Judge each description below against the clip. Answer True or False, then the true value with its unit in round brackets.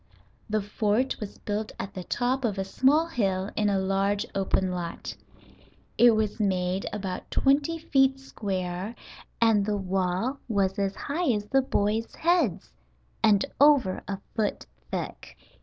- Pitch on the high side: True (210 Hz)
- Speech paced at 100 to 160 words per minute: True (145 wpm)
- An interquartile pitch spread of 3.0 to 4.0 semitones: False (4.8 semitones)